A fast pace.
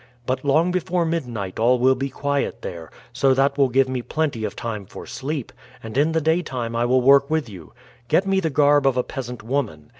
Yes: fast, 215 wpm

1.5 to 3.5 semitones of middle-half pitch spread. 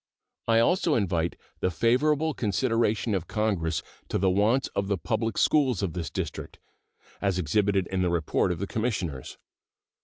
No: average, 4.4 semitones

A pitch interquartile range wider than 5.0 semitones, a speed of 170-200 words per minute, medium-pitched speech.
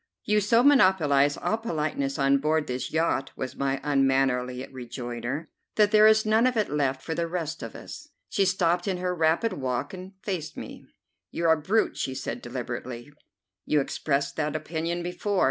Yes: wide, 5.6 semitones; average, 175 wpm; medium, 160 Hz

